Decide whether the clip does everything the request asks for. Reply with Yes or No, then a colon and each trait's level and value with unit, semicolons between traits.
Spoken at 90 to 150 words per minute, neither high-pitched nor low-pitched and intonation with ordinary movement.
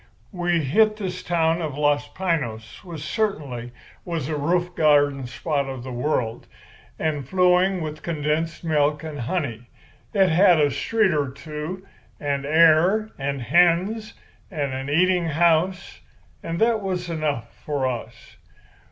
Yes: average, 140 wpm; medium, 155 Hz; average, 3.9 semitones